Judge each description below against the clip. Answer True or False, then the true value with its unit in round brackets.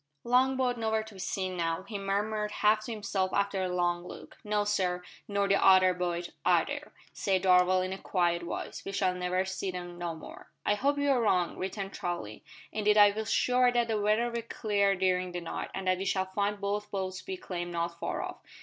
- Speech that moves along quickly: True (215 wpm)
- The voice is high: True (195 Hz)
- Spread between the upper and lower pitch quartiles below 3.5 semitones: True (2.7 semitones)